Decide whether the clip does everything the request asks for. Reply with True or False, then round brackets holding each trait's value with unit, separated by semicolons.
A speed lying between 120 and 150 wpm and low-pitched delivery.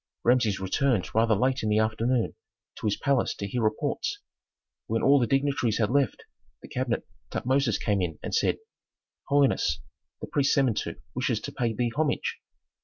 False (165 wpm; 120 Hz)